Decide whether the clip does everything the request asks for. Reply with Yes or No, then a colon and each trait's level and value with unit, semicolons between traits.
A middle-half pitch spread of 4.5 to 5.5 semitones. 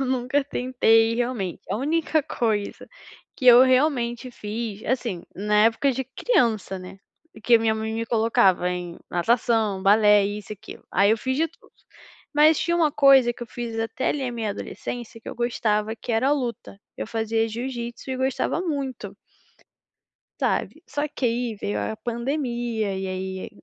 No: average, 3.5 semitones